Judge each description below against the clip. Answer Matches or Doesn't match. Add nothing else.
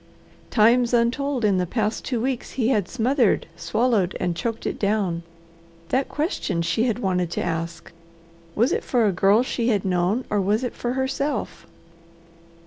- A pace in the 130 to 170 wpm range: Matches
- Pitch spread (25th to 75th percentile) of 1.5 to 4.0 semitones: Doesn't match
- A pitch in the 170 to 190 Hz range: Doesn't match